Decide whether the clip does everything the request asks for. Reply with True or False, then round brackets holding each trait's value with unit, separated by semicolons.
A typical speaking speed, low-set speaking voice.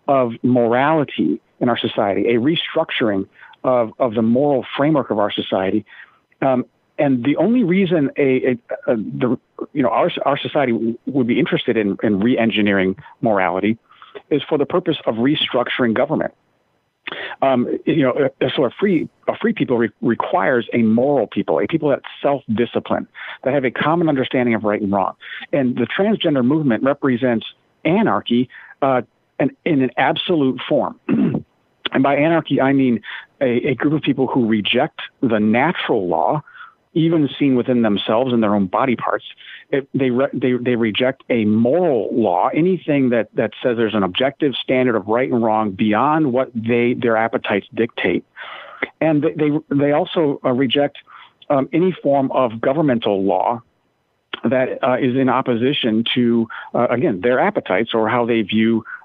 True (165 wpm; 125 Hz)